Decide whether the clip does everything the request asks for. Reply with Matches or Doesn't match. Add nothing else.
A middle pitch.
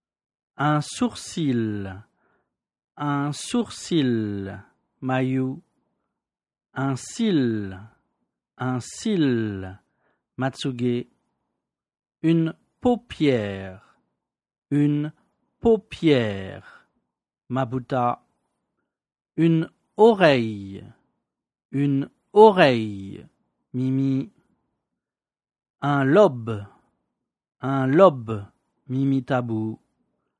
Doesn't match